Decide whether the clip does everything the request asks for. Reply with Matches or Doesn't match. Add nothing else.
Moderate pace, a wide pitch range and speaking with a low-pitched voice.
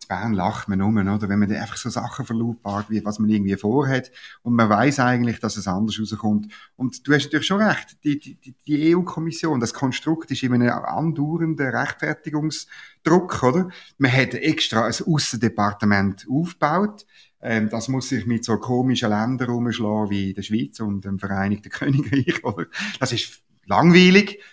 Matches